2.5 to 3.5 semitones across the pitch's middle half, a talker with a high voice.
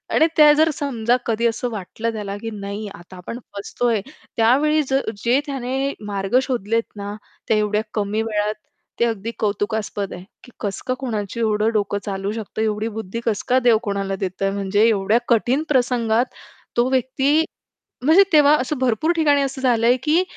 No: average, 3.9 semitones; high, 225 Hz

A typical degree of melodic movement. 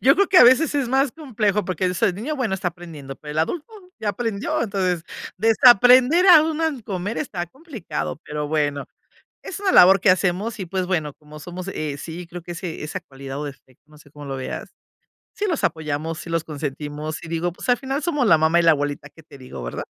No: wide, 8.2 semitones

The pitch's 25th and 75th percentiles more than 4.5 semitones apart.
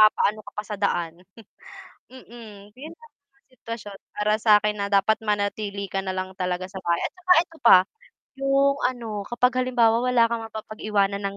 No: average, 3.3 semitones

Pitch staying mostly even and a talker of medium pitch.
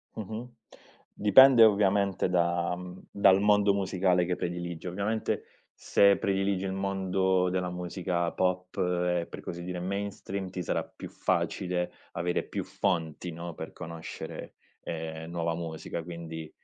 No: narrow, 2.1 semitones; very low, 90 Hz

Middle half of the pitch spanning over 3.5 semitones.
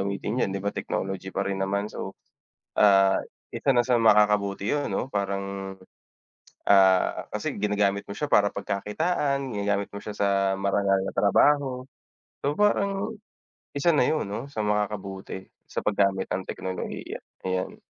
Yes: average, 4.1 semitones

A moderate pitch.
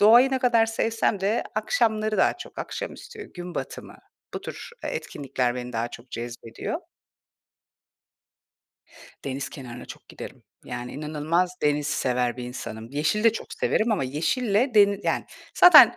Yes: medium, 170 Hz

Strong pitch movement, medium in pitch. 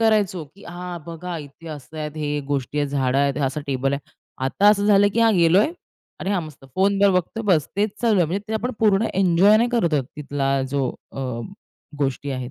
Yes: wide, 6.1 semitones; medium, 170 Hz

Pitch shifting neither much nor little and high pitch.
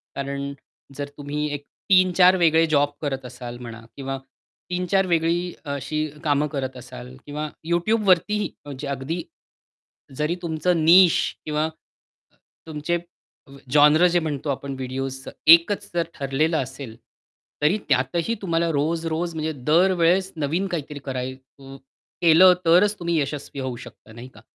No: average, 3.8 semitones; medium, 155 Hz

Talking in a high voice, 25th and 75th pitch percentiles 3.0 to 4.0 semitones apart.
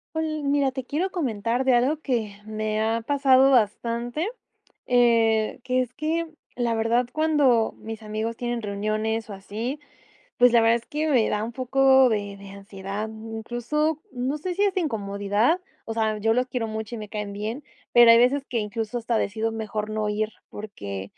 Yes: high, 230 Hz; average, 3.5 semitones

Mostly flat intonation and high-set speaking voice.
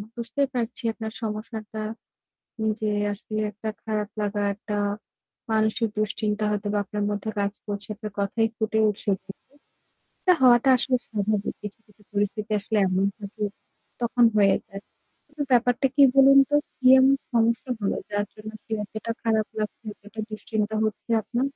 Yes: narrow, 2.1 semitones; high, 215 Hz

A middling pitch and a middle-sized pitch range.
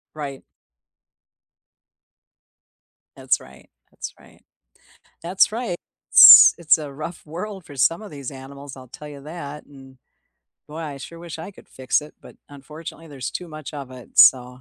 Yes: medium, 150 Hz; average, 3.3 semitones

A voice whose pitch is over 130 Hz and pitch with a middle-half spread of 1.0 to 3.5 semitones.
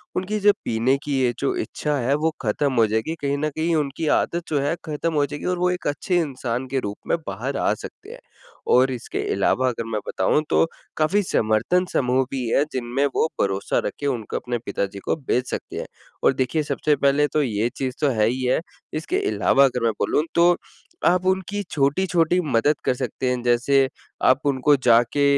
No: medium, 140 Hz; average, 4.0 semitones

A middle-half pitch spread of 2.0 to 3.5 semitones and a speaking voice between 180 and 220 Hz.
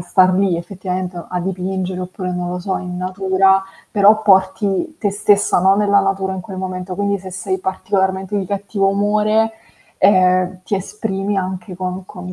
No: narrow, 1.5 semitones; high, 190 Hz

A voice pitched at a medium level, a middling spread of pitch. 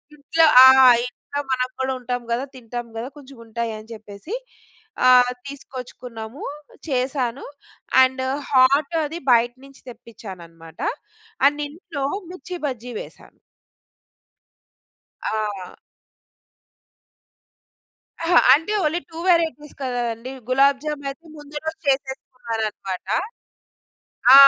No: very high, 255 Hz; average, 3.6 semitones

